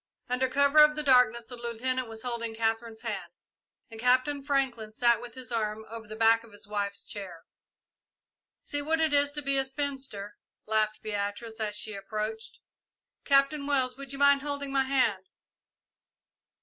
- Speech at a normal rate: Yes, average, 165 wpm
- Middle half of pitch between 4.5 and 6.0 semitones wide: No, average, 4.0 semitones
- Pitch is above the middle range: Yes, high, 240 Hz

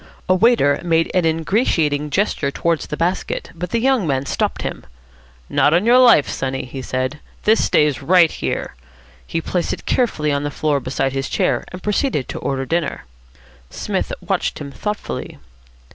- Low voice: No, medium, 160 Hz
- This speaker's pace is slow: No, average, 170 wpm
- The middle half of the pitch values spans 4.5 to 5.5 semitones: Yes, average, 4.8 semitones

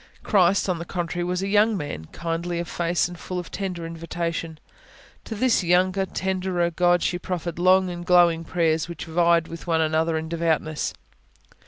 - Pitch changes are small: Yes, narrow, 1.6 semitones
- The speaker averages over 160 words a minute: Yes, average, 175 wpm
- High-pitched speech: No, medium, 175 Hz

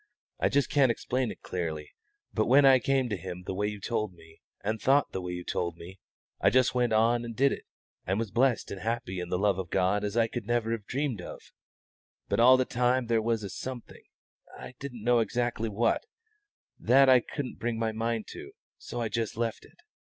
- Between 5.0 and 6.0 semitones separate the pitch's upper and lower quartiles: No, average, 3.6 semitones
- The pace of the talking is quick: Yes, fast, 220 wpm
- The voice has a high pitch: No, low, 115 Hz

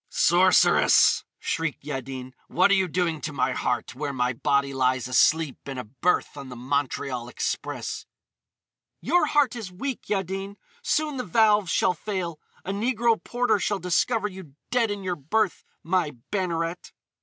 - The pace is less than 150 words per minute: No, average, 155 wpm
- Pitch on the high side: No, medium, 175 Hz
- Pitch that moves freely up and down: Yes, wide, 7.0 semitones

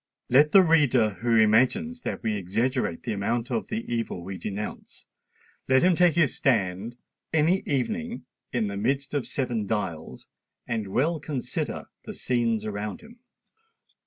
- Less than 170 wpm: Yes, average, 145 wpm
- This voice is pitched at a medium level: No, low, 120 Hz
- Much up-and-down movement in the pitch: Yes, wide, 6.0 semitones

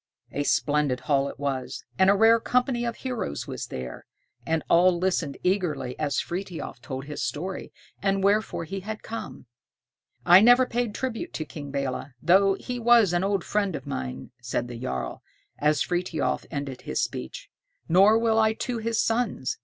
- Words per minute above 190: No, average, 170 wpm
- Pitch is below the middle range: No, medium, 185 Hz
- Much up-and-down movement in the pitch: Yes, wide, 7.5 semitones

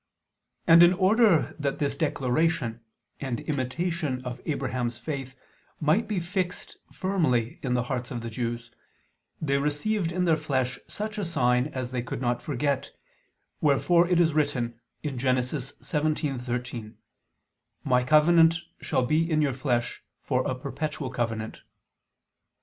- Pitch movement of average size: Yes, average, 4.7 semitones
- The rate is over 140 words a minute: No, slow, 135 wpm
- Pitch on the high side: No, medium, 140 Hz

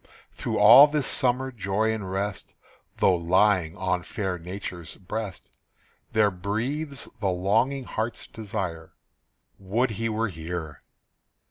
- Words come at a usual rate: No, slow, 120 wpm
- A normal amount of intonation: Yes, average, 3.9 semitones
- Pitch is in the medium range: No, low, 100 Hz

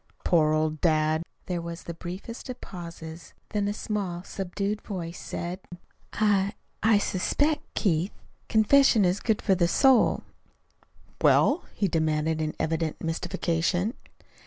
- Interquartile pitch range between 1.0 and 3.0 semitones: No, average, 4.2 semitones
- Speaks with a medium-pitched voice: Yes, medium, 180 Hz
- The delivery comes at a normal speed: No, slow, 130 wpm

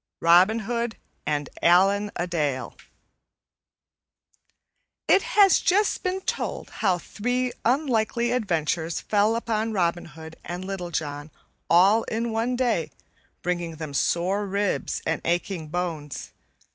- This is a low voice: No, high, 190 Hz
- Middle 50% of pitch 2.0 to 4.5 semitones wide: No, average, 5.2 semitones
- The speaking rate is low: Yes, slow, 120 wpm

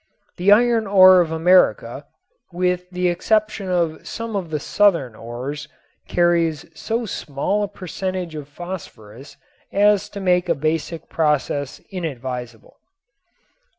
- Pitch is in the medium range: Yes, medium, 175 Hz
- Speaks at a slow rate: Yes, slow, 120 wpm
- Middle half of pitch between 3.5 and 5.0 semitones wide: Yes, average, 4.3 semitones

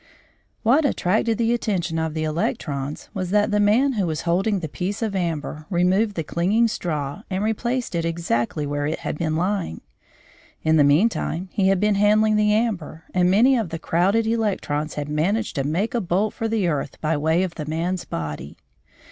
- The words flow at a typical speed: Yes, average, 190 wpm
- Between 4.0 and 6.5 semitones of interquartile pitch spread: Yes, average, 5.1 semitones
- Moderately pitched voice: Yes, medium, 180 Hz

